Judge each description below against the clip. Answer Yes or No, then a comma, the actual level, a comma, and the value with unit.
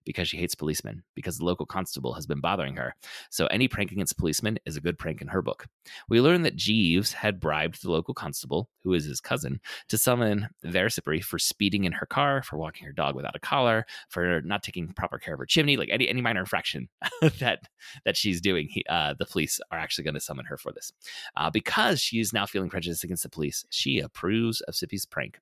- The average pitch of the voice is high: No, low, 105 Hz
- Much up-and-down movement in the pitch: Yes, wide, 6.0 semitones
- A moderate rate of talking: No, fast, 225 wpm